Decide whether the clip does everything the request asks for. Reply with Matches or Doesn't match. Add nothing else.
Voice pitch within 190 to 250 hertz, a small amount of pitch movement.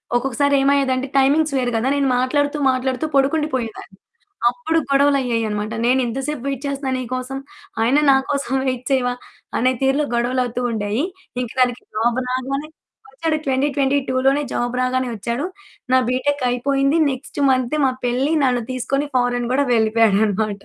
Doesn't match